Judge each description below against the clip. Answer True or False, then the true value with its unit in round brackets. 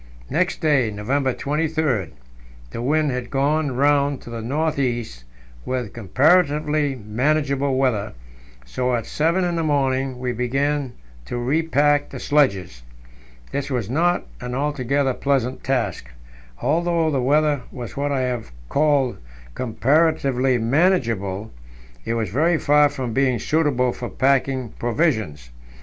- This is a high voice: False (135 Hz)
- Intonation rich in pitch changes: False (3.5 semitones)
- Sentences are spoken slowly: True (130 wpm)